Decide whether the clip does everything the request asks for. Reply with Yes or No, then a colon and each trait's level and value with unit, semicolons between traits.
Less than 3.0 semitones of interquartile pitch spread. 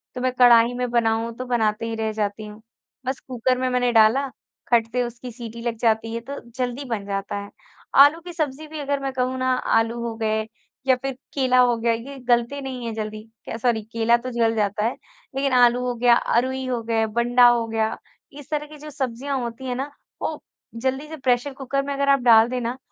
Yes: narrow, 2.5 semitones